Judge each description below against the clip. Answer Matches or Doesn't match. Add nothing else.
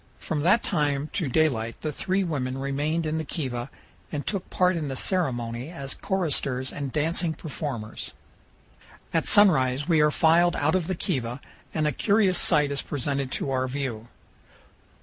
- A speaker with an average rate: Matches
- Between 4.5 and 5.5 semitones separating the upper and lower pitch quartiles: Doesn't match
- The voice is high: Doesn't match